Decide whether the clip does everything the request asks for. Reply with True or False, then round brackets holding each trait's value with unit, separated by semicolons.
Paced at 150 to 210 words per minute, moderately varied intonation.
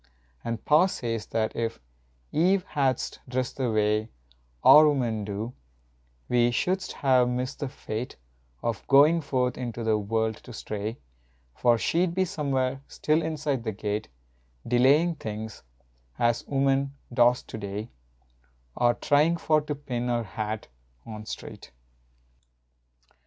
False (135 wpm; 4.5 semitones)